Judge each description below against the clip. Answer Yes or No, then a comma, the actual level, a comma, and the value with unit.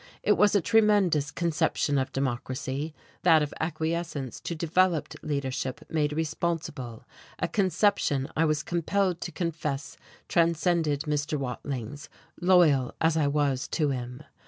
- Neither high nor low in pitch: Yes, medium, 155 Hz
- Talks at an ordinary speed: No, slow, 130 wpm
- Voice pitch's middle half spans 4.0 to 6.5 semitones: No, average, 3.5 semitones